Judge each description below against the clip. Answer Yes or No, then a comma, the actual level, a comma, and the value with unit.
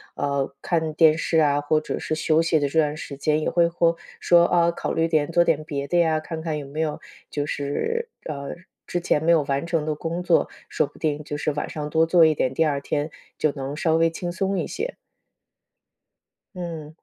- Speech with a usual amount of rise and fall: No, narrow, 2.3 semitones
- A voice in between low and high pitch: Yes, medium, 155 Hz